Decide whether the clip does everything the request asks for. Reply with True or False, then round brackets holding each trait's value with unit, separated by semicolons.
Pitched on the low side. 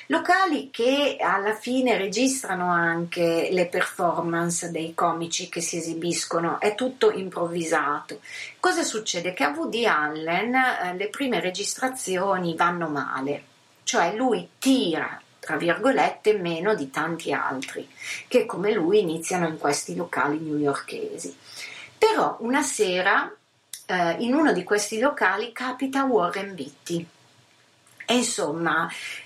False (185 Hz)